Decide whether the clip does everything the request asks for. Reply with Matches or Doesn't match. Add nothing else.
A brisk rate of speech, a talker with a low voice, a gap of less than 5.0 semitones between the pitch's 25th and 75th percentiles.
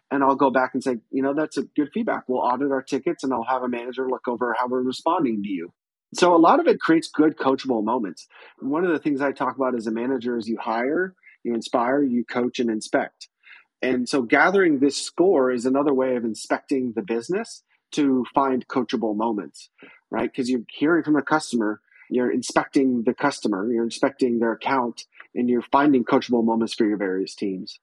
Matches